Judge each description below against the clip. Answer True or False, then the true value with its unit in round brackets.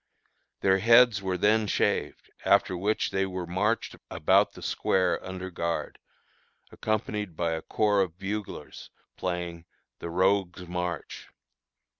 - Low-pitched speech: True (95 Hz)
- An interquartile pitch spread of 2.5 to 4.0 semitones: True (2.8 semitones)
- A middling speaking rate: False (125 wpm)